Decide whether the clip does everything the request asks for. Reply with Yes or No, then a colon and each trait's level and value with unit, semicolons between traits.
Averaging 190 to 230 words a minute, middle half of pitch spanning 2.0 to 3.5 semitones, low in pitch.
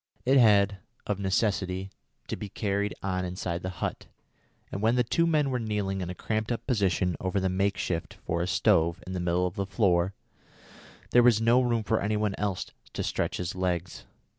Yes: average, 200 wpm; average, 3.1 semitones; low, 100 Hz